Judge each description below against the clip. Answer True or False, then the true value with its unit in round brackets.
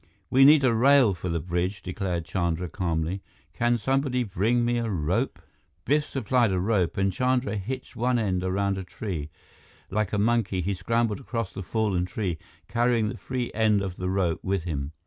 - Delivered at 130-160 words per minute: False (185 wpm)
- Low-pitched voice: True (100 Hz)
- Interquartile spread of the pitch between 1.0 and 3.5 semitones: False (4.7 semitones)